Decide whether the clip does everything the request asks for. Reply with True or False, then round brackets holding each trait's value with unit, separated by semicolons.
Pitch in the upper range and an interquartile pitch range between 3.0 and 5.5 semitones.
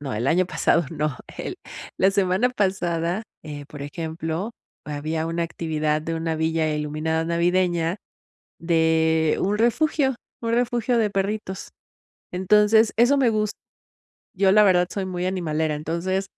False (175 Hz; 3.9 semitones)